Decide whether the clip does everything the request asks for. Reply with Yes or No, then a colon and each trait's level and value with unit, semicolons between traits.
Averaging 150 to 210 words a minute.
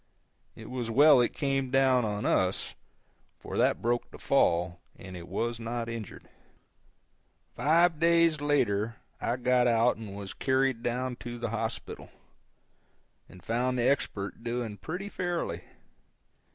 No: average, 140 wpm